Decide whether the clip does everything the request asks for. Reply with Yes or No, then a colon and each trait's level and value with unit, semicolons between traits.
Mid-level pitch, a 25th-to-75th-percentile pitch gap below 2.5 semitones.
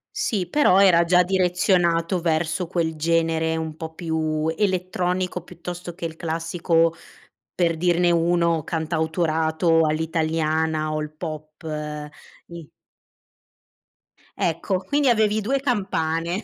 Yes: medium, 170 Hz; narrow, 2.0 semitones